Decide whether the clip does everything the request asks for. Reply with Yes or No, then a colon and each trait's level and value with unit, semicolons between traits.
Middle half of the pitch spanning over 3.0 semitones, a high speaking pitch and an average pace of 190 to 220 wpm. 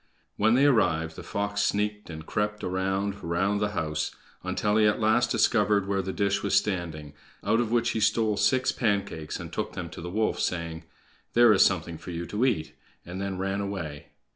No: average, 3.4 semitones; low, 100 Hz; average, 195 wpm